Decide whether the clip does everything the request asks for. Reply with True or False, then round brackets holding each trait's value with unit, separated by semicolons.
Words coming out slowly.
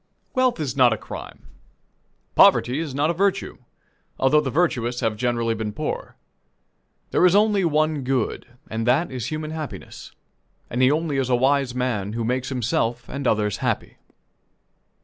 False (160 wpm)